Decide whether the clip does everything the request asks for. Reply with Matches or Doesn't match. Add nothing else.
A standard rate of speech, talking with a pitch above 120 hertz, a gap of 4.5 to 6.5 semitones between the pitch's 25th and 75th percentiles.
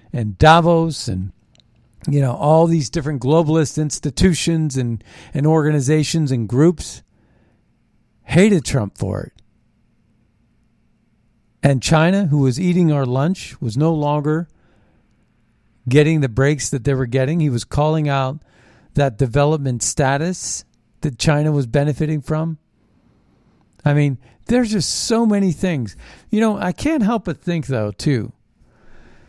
Doesn't match